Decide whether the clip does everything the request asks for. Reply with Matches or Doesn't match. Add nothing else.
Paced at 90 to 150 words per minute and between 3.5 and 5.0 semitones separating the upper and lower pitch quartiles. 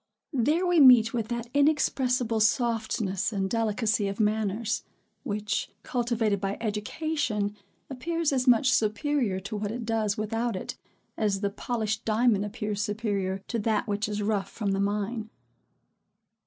Doesn't match